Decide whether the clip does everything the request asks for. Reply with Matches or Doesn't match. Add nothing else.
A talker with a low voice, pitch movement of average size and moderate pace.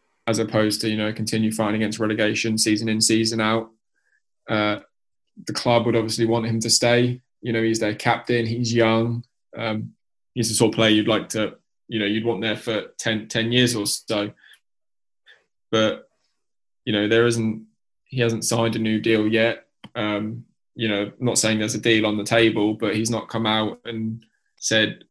Doesn't match